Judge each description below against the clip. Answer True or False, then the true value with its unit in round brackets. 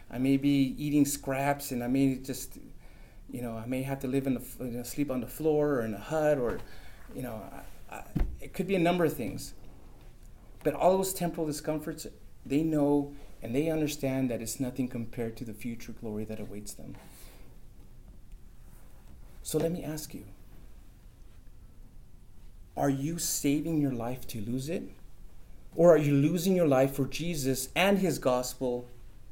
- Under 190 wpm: True (170 wpm)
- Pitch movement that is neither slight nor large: True (4.0 semitones)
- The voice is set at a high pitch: False (135 Hz)